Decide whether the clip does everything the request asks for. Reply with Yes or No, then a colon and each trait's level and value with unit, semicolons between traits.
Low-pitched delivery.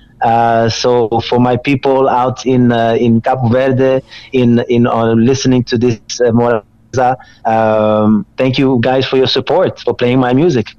Yes: low, 120 Hz